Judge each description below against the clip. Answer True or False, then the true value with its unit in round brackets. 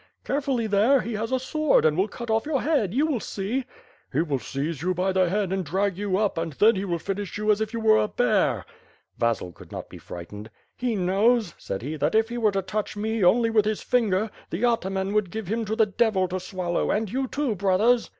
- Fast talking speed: True (235 wpm)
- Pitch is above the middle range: True (210 Hz)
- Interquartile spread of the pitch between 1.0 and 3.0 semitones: False (3.6 semitones)